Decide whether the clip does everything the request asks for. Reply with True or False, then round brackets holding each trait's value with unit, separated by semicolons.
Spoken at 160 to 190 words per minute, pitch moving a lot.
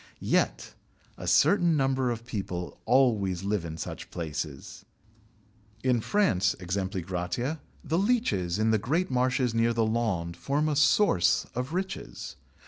False (135 wpm; 6.8 semitones)